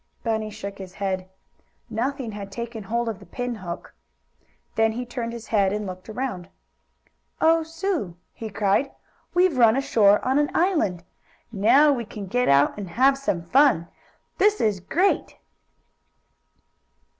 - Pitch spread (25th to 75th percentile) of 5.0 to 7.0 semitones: Yes, average, 5.3 semitones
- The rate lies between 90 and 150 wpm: Yes, average, 145 wpm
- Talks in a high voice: Yes, high, 225 Hz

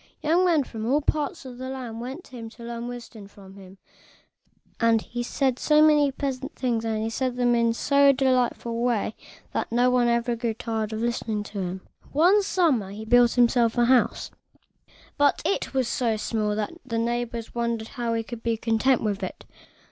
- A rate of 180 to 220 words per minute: Yes, average, 195 wpm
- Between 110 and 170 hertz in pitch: No, high, 235 Hz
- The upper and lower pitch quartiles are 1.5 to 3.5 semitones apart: Yes, narrow, 2.6 semitones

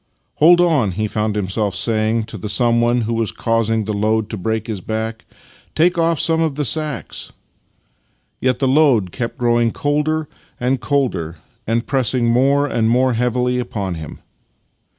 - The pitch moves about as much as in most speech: Yes, average, 3.9 semitones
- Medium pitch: No, low, 115 Hz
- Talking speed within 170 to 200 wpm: Yes, average, 175 wpm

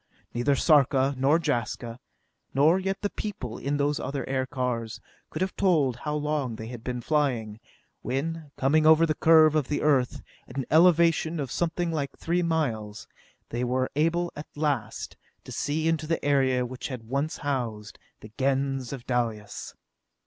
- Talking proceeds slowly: No, average, 165 wpm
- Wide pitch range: No, average, 4.0 semitones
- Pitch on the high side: No, medium, 140 Hz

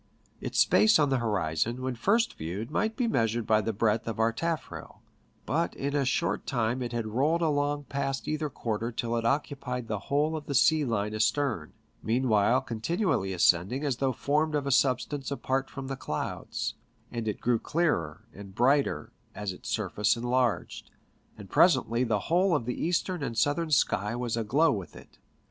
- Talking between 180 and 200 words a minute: Yes, average, 185 wpm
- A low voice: Yes, low, 125 Hz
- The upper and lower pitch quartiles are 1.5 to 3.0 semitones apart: No, average, 4.5 semitones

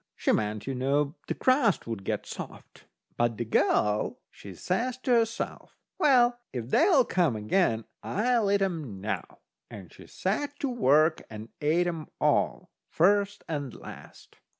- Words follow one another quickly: No, average, 150 wpm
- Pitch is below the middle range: No, medium, 160 Hz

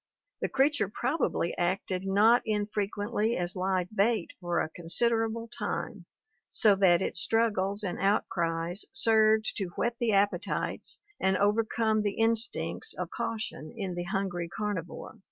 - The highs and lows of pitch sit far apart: No, average, 3.4 semitones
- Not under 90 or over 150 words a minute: Yes, slow, 135 wpm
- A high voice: Yes, high, 205 Hz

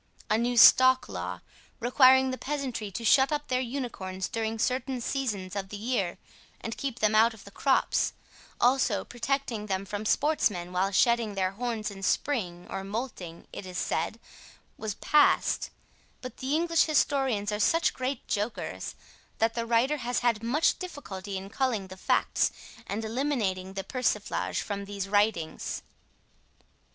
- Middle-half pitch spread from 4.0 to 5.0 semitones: Yes, average, 4.5 semitones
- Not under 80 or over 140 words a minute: No, average, 155 wpm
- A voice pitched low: No, high, 230 Hz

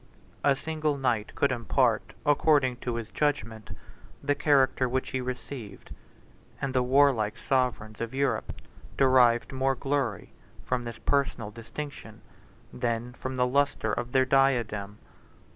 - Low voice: Yes, low, 130 Hz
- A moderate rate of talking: No, slow, 130 wpm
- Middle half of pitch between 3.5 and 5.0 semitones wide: No, average, 3.0 semitones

